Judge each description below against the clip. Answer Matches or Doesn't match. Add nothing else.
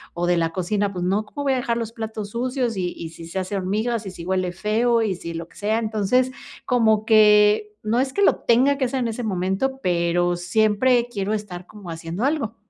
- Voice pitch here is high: Matches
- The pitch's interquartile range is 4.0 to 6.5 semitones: Matches